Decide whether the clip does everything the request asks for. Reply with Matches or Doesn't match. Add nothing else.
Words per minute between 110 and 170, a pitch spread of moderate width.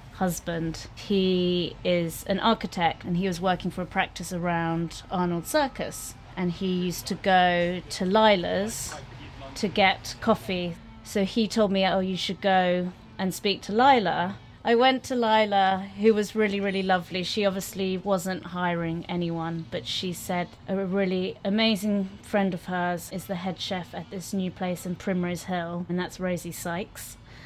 Doesn't match